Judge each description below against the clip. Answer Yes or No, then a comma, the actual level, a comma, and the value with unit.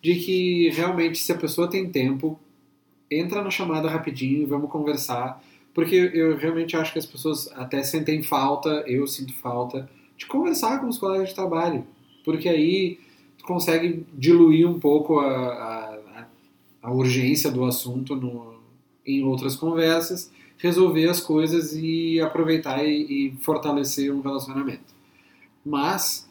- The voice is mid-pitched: Yes, medium, 155 Hz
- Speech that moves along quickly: No, average, 140 wpm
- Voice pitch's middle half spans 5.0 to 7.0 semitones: No, average, 3.6 semitones